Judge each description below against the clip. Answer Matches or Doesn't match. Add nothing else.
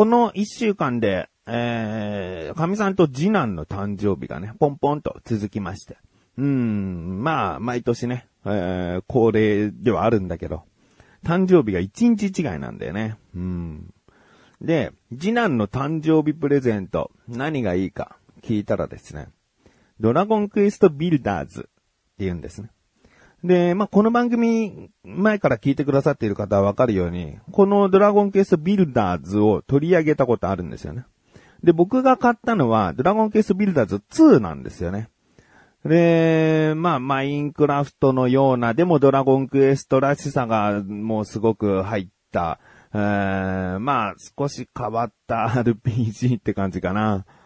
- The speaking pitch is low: Matches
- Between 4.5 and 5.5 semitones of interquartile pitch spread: Doesn't match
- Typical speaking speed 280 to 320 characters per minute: Matches